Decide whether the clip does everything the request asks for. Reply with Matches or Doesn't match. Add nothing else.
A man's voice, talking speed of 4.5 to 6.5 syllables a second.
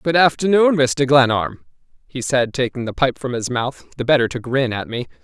Matches